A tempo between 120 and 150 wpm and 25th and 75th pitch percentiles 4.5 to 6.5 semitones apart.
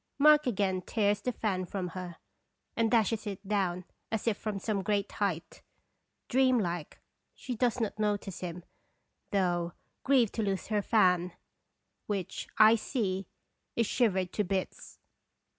No: average, 140 wpm; average, 3.3 semitones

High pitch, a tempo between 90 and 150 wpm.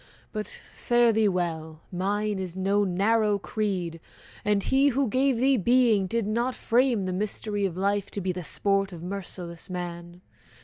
No: high, 200 Hz; average, 165 wpm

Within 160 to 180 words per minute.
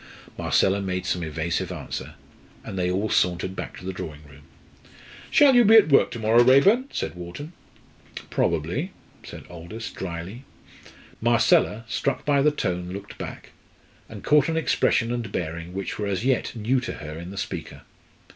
Yes: average, 165 wpm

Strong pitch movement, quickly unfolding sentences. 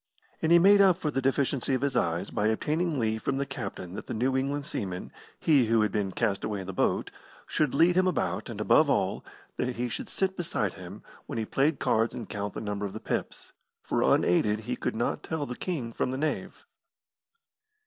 Yes: wide, 6.1 semitones; fast, 220 wpm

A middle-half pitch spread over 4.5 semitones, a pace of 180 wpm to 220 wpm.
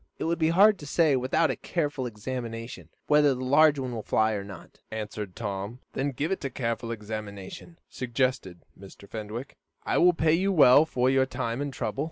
Yes: average, 5.2 semitones; average, 190 wpm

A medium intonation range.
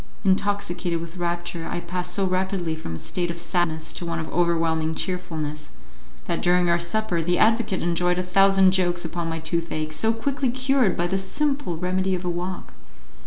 No: narrow, 2.1 semitones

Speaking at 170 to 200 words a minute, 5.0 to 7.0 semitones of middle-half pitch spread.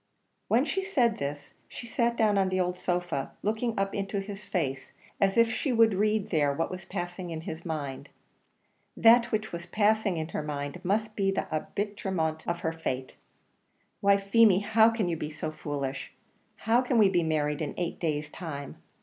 Yes: average, 185 wpm; wide, 5.4 semitones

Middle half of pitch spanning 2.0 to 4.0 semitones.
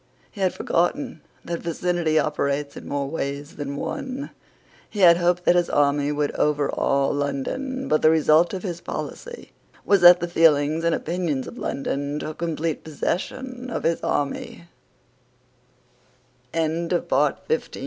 Yes: average, 3.6 semitones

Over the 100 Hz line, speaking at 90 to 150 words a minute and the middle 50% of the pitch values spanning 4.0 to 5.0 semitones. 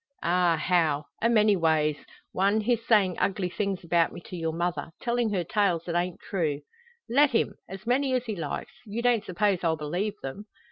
No: medium, 185 Hz; average, 190 wpm; average, 4.4 semitones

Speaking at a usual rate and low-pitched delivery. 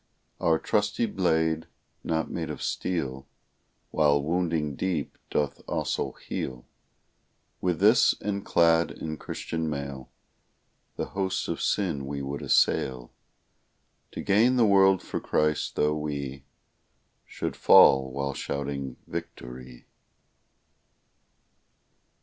No: slow, 110 wpm; very low, 75 Hz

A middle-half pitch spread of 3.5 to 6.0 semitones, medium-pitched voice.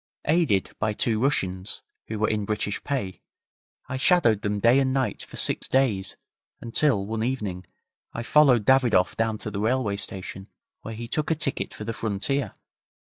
No: average, 4.4 semitones; low, 115 Hz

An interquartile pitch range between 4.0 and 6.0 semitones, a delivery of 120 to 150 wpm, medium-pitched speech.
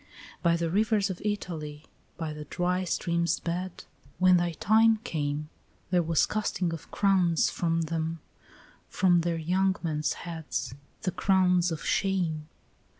No: narrow, 2.5 semitones; average, 140 wpm; medium, 170 Hz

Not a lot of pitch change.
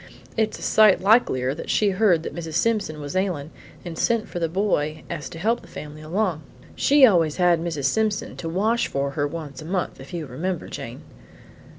No: average, 5.2 semitones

